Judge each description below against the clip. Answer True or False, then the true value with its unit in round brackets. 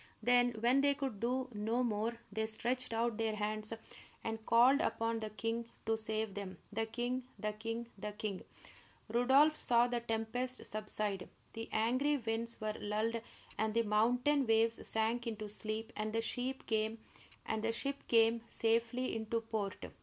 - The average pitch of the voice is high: True (225 Hz)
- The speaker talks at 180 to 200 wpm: False (150 wpm)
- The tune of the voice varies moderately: False (2.0 semitones)